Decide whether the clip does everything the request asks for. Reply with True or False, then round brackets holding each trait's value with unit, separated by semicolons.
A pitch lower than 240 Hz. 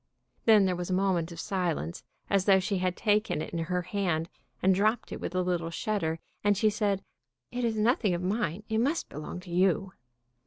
True (190 Hz)